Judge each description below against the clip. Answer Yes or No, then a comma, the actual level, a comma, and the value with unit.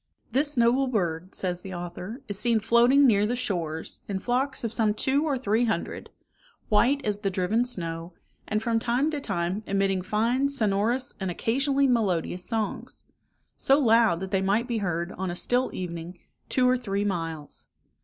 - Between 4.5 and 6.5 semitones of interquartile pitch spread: Yes, average, 4.9 semitones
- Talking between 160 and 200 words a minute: Yes, average, 175 wpm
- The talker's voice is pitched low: No, high, 215 Hz